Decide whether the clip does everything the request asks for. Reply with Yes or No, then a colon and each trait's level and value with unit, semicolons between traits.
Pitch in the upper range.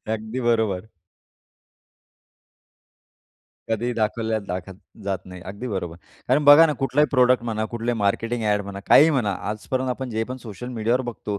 No: low, 115 Hz